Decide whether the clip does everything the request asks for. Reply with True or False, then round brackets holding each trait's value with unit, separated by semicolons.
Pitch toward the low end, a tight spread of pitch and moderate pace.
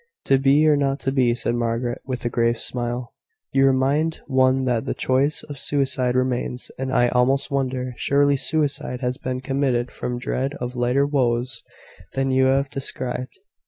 True (130 Hz; 1.8 semitones; 170 wpm)